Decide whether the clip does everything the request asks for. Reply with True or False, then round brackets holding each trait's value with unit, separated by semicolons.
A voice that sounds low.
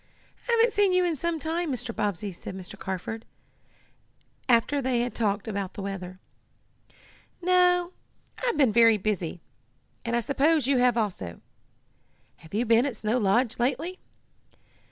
False (240 Hz)